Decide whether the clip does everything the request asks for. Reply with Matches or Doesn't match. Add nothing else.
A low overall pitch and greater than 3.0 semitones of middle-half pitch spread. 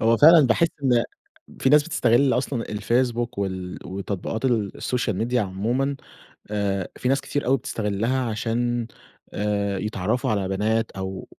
Matches